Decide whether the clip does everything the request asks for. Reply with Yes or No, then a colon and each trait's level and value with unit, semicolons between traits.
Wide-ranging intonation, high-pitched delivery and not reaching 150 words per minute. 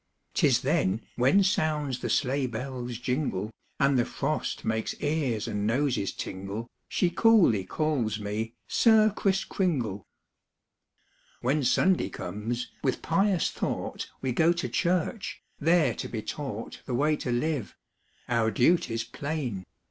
No: wide, 6.1 semitones; low, 130 Hz; average, 140 wpm